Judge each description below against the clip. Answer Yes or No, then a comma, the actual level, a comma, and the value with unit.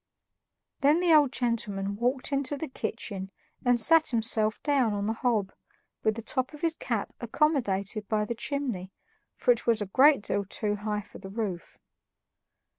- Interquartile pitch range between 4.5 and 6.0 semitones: Yes, average, 5.0 semitones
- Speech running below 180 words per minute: Yes, average, 170 wpm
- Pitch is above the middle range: Yes, high, 230 Hz